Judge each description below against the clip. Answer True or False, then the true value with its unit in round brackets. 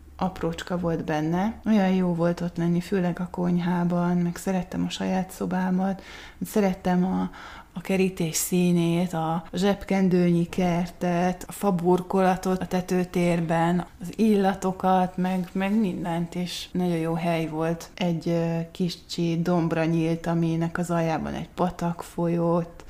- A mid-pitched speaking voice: True (175 Hz)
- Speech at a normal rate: True (125 wpm)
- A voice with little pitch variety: True (1.7 semitones)